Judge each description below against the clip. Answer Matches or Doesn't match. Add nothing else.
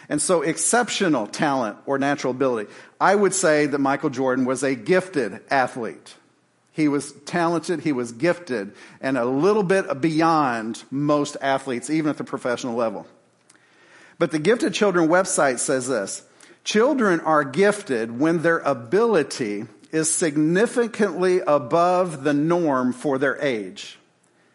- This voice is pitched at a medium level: Matches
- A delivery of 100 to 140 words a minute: Matches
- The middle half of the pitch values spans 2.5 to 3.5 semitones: Doesn't match